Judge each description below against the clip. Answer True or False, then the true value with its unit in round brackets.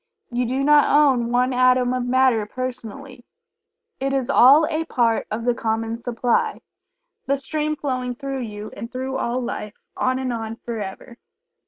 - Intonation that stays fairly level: True (2.3 semitones)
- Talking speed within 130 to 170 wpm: True (160 wpm)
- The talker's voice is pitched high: True (250 Hz)